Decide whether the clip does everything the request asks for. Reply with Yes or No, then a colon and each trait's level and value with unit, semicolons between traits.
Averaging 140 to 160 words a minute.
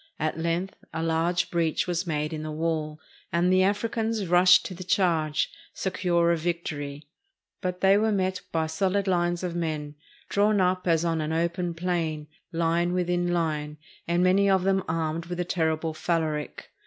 No: average, 175 wpm